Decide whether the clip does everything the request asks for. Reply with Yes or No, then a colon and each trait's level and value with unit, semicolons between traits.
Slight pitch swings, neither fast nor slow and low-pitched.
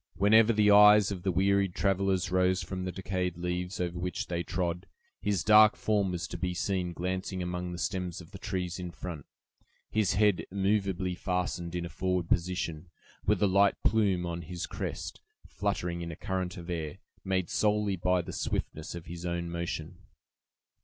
Yes: narrow, 2.0 semitones; average, 180 wpm; very low, 90 Hz